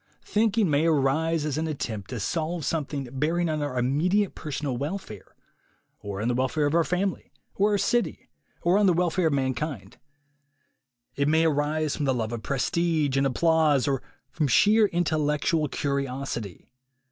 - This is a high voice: No, medium, 150 Hz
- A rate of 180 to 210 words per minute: No, average, 165 wpm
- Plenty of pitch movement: No, average, 3.8 semitones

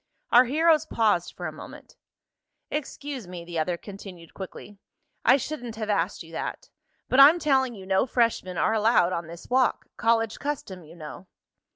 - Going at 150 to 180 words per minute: Yes, average, 170 wpm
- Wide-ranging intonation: Yes, wide, 6.5 semitones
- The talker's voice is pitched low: No, high, 215 Hz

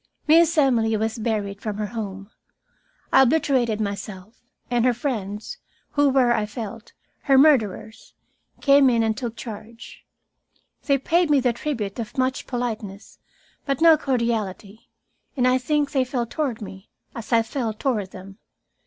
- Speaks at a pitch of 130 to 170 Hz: No, high, 235 Hz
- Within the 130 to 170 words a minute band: Yes, average, 150 wpm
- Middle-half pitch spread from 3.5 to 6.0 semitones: Yes, average, 3.9 semitones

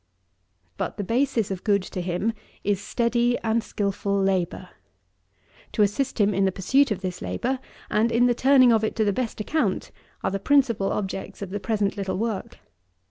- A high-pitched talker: Yes, high, 210 Hz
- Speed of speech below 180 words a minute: No, average, 190 wpm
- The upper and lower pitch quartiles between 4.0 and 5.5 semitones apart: No, average, 3.5 semitones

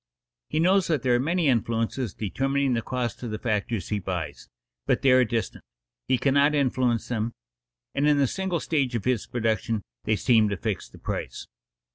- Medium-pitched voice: No, low, 125 Hz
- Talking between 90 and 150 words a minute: No, average, 185 wpm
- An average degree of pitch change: Yes, average, 4.1 semitones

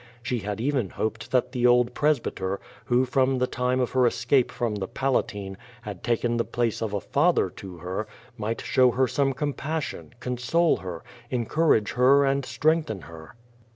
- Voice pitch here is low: Yes, low, 125 Hz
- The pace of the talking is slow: No, average, 180 wpm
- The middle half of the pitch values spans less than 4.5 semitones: Yes, average, 4.1 semitones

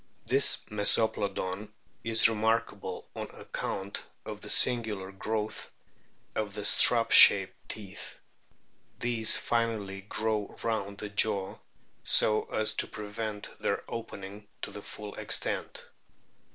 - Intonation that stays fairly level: Yes, narrow, 1.9 semitones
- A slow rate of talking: Yes, slow, 110 wpm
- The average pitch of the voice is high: No, low, 105 Hz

